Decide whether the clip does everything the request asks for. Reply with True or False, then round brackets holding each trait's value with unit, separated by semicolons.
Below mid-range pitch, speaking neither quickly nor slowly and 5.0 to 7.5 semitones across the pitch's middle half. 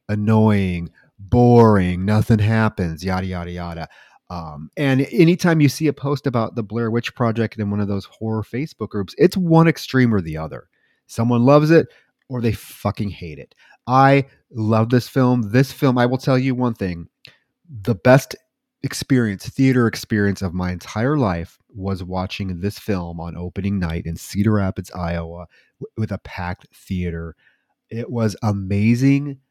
True (110 Hz; 165 wpm; 5.3 semitones)